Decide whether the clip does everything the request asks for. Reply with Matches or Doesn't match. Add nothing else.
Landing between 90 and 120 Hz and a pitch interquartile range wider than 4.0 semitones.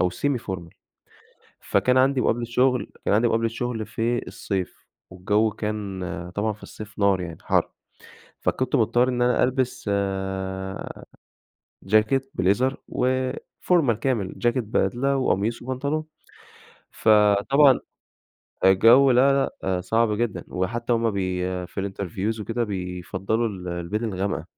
Matches